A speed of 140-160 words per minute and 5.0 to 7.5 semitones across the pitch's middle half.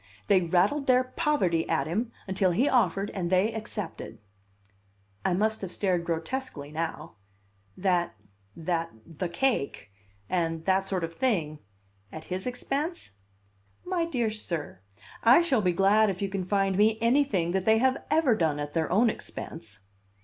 Yes: average, 155 wpm; wide, 5.6 semitones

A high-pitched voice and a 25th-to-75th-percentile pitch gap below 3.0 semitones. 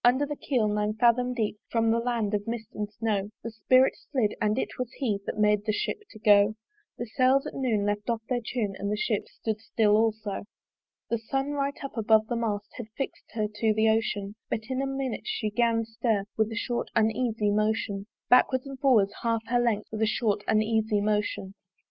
Yes: high, 220 Hz; narrow, 2.4 semitones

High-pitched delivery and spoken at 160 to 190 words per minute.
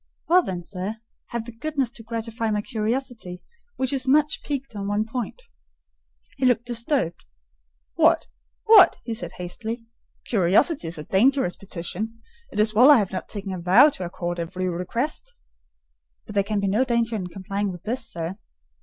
Yes: high, 220 Hz; average, 170 wpm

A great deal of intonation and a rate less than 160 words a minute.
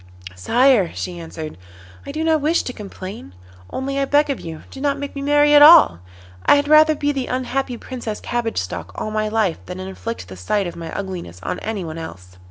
No: wide, 8.5 semitones; fast, 205 wpm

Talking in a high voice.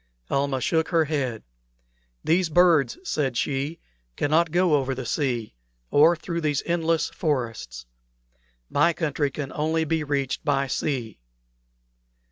No: medium, 150 Hz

